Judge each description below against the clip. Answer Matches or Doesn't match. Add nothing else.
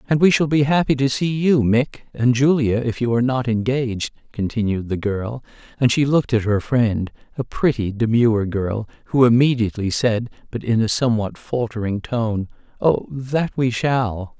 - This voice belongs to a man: Matches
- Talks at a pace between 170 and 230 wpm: Matches